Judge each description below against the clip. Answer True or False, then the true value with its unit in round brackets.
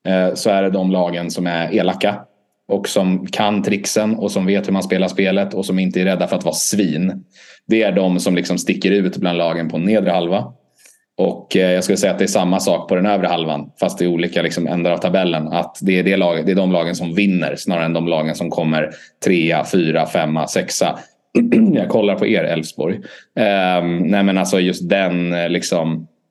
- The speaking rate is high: True (210 wpm)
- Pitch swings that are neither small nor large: False (1.8 semitones)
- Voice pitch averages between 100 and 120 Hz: False (90 Hz)